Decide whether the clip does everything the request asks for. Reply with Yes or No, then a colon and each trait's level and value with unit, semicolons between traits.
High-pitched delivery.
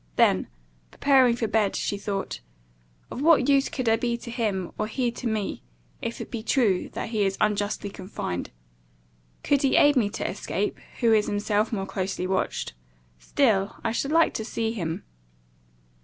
Yes: high, 220 Hz